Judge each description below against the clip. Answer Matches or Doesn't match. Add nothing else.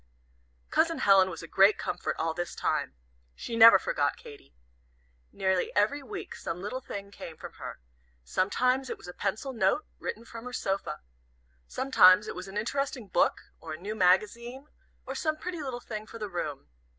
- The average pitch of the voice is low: Doesn't match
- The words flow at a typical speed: Matches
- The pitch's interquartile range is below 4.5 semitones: Doesn't match